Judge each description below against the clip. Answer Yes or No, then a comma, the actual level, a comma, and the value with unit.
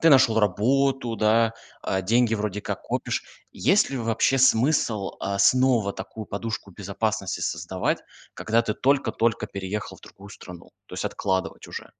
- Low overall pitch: Yes, low, 110 Hz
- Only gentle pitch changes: No, average, 3.2 semitones